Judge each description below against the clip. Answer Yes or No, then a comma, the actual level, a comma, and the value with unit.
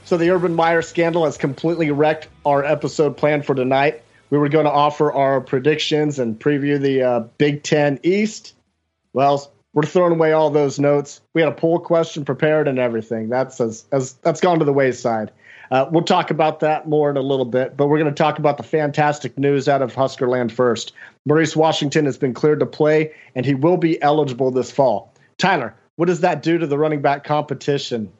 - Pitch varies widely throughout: No, average, 2.7 semitones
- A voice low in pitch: No, medium, 145 Hz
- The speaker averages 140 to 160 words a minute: No, fast, 205 wpm